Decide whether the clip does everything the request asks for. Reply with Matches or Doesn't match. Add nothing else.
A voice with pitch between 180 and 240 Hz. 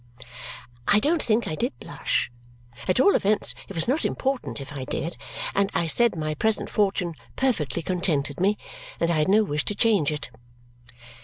Matches